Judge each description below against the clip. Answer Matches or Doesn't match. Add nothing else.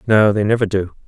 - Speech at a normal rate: Doesn't match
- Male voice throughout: Matches